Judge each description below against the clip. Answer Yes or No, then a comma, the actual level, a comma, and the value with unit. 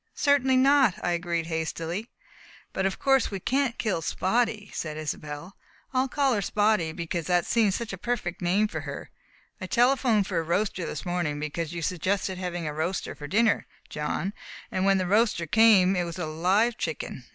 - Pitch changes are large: No, average, 4.9 semitones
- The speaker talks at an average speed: Yes, average, 185 wpm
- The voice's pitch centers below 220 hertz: Yes, medium, 185 Hz